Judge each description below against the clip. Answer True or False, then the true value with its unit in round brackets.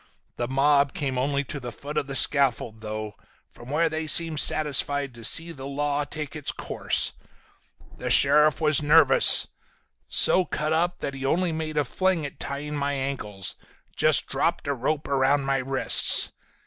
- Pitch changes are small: True (2.2 semitones)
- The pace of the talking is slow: False (170 wpm)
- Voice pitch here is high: False (145 Hz)